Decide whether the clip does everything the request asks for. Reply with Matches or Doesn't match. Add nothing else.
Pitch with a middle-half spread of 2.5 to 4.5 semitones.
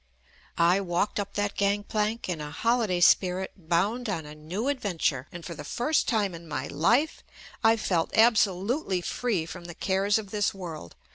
Matches